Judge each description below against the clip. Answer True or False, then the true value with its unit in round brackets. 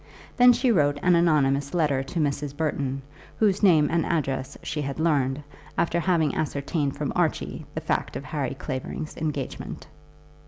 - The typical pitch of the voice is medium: True (150 Hz)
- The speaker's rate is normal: True (155 wpm)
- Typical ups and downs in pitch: True (3.3 semitones)